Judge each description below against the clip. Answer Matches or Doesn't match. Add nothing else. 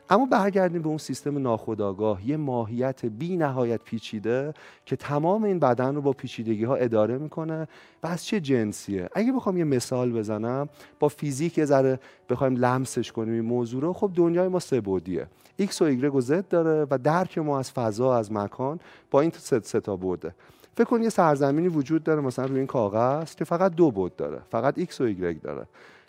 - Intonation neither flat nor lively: Doesn't match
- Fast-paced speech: Matches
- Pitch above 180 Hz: Doesn't match